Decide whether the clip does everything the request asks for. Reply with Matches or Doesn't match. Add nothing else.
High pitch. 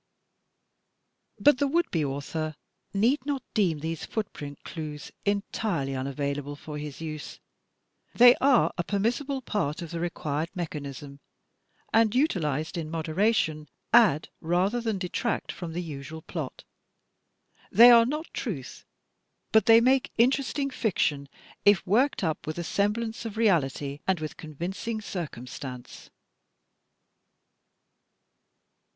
Doesn't match